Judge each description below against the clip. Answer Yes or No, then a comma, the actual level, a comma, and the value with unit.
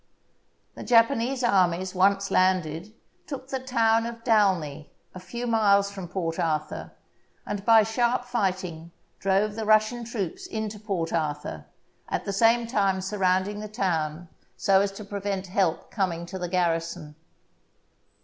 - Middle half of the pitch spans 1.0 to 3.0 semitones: No, average, 3.8 semitones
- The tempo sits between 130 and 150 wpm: Yes, average, 140 wpm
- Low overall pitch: No, high, 195 Hz